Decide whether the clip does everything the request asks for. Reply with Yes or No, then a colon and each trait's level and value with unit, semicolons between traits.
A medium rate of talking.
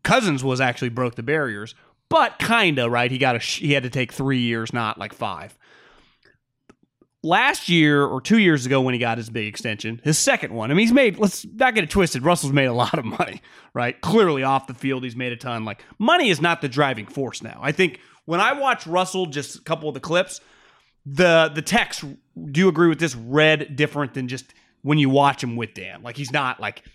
No: fast, 225 wpm